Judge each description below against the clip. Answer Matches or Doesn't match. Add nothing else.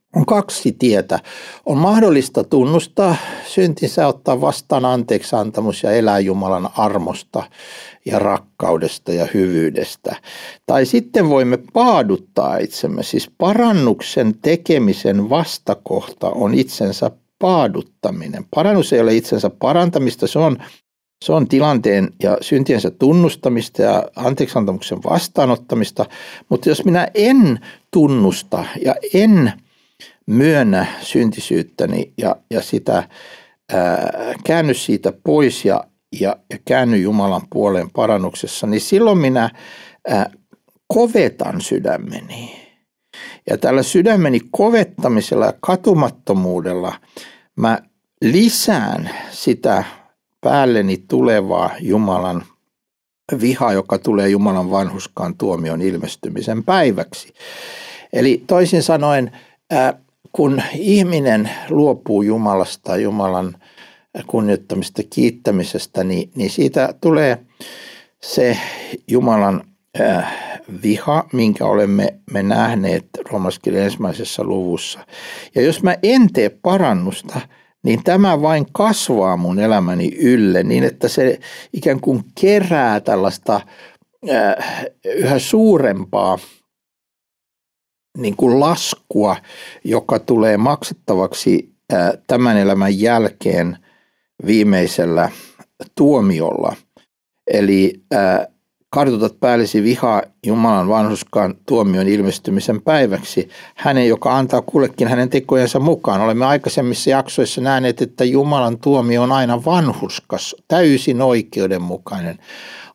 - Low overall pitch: Matches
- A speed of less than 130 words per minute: Matches